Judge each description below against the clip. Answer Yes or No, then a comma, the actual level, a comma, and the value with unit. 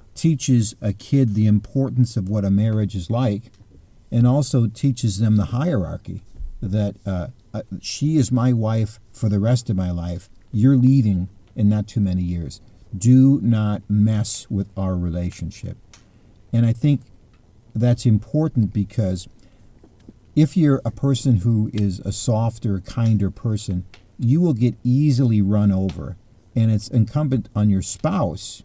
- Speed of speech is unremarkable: Yes, average, 145 wpm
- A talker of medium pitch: No, low, 110 Hz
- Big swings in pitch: No, average, 3.7 semitones